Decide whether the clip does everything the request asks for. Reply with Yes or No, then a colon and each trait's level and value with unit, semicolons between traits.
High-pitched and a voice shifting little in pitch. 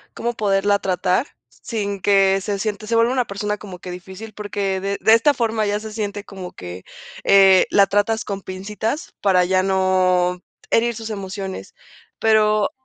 Yes: high, 200 Hz; narrow, 2.3 semitones